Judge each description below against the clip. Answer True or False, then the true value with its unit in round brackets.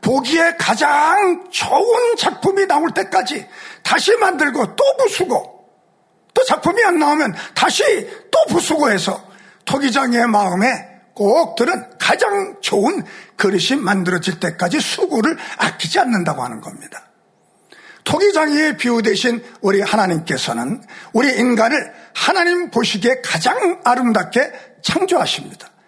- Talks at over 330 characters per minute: False (275 characters per minute)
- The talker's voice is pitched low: False (275 Hz)